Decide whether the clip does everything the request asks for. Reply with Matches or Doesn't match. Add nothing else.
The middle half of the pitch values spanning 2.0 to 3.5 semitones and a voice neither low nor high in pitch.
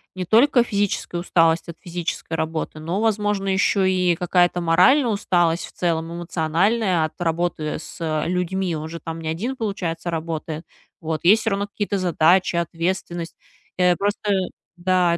Matches